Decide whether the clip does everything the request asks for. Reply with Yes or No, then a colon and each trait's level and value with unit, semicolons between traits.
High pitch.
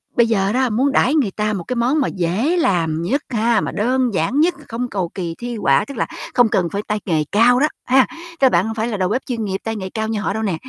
Yes: high, 225 Hz